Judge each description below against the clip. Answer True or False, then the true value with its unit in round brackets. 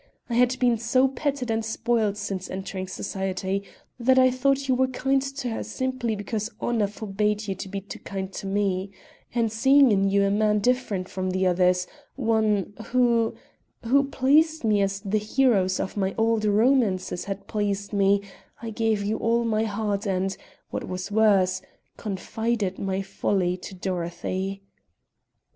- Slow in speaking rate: False (160 wpm)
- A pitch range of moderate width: True (3.5 semitones)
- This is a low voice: False (210 Hz)